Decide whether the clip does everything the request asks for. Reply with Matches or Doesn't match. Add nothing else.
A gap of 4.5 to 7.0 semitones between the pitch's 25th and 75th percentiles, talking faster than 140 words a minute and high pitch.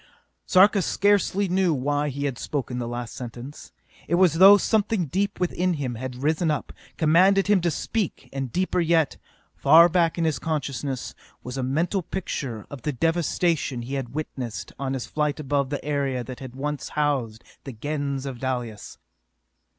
Doesn't match